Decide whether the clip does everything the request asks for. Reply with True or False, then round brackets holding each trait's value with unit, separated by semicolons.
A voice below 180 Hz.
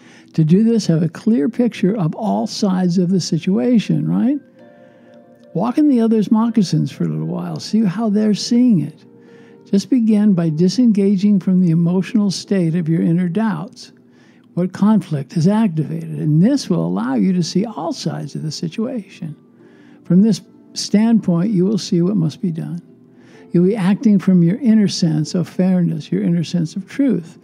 False (190 Hz)